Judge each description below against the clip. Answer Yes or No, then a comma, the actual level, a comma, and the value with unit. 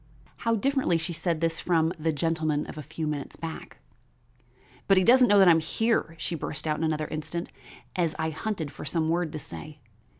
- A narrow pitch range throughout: Yes, narrow, 2.2 semitones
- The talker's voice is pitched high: No, medium, 165 Hz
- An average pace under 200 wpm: No, fast, 205 wpm